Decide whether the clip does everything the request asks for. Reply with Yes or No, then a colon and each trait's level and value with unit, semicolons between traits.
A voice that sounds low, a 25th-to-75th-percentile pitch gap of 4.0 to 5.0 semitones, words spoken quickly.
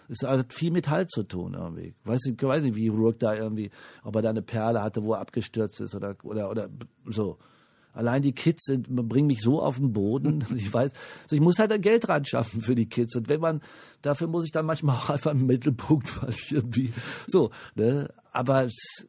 Yes: low, 130 Hz; average, 4.5 semitones; fast, 220 wpm